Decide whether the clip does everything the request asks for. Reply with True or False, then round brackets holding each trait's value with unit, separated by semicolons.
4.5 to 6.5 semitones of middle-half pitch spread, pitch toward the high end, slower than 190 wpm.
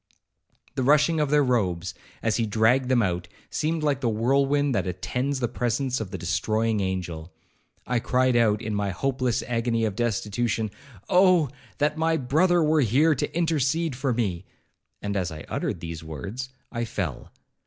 False (5.6 semitones; 120 Hz; 165 wpm)